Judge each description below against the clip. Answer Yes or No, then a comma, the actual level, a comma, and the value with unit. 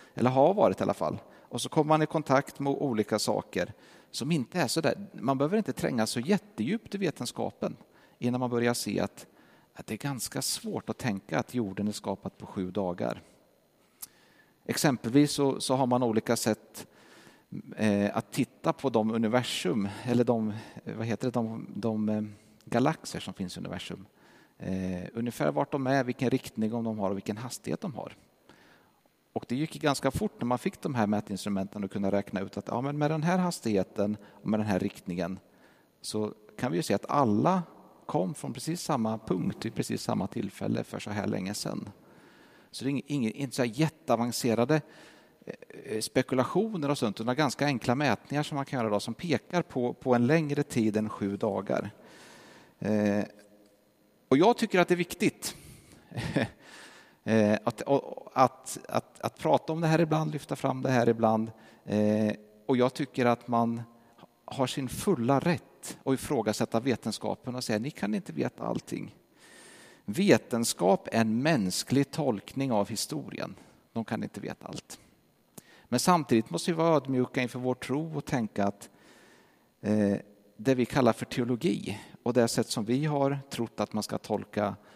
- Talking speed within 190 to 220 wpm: No, average, 175 wpm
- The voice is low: Yes, low, 120 Hz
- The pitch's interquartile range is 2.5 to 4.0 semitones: No, average, 4.6 semitones